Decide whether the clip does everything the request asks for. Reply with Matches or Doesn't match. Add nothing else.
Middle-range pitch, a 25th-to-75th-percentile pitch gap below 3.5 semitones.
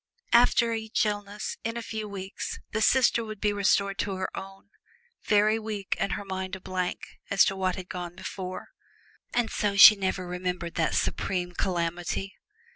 Doesn't match